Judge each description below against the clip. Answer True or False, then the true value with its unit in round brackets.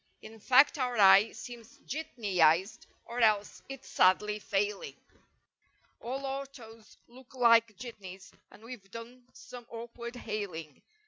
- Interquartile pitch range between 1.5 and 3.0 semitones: False (3.4 semitones)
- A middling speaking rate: False (120 wpm)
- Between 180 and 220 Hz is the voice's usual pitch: False (230 Hz)